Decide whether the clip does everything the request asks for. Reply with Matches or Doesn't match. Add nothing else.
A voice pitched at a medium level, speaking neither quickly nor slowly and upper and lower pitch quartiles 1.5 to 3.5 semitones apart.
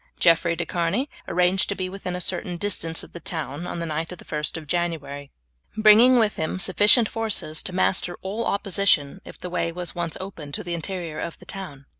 Doesn't match